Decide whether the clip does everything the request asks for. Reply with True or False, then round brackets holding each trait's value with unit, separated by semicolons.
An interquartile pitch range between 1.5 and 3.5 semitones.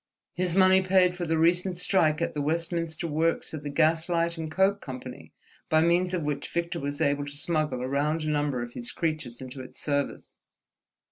True (3.1 semitones)